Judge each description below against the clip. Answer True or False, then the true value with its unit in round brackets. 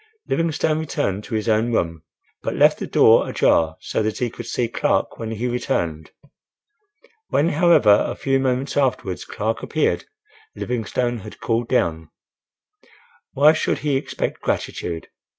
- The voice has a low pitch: True (120 Hz)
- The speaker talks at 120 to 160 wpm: True (145 wpm)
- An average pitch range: True (4.5 semitones)